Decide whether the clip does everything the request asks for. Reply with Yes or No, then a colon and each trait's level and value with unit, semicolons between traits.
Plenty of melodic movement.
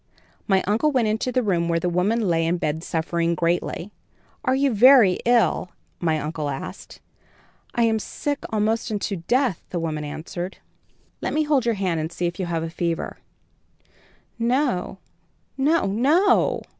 Yes: wide, 6.3 semitones